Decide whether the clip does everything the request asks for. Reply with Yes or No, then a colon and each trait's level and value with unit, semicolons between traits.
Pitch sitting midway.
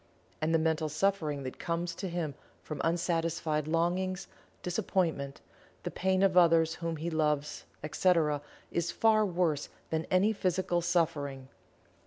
Yes: medium, 165 Hz